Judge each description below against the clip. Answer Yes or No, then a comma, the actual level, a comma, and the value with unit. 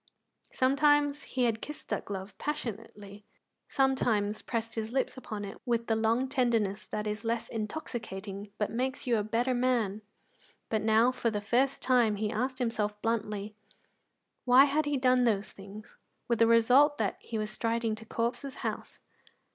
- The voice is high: Yes, high, 230 Hz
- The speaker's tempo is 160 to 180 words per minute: Yes, average, 165 wpm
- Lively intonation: No, average, 3.1 semitones